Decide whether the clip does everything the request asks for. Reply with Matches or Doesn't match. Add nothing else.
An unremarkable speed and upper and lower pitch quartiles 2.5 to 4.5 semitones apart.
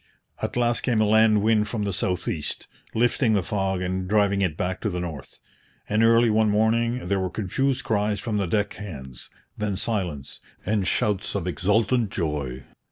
Matches